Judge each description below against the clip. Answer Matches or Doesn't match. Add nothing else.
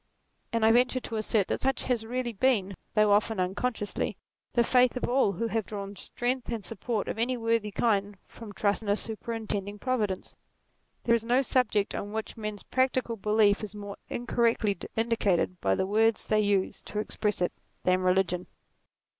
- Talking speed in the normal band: Matches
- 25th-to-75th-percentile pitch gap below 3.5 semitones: Matches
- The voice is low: Doesn't match